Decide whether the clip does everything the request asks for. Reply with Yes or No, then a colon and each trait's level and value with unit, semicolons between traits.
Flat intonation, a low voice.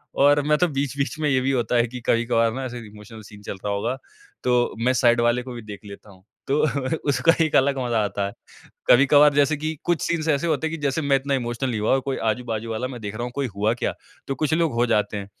No: average, 3.8 semitones; low, 125 Hz